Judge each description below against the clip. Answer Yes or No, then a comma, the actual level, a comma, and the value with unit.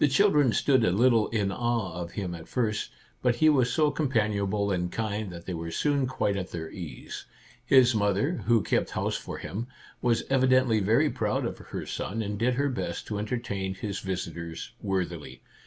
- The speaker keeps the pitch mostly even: No, average, 4.8 semitones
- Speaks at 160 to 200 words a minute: Yes, average, 190 wpm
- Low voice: Yes, low, 105 Hz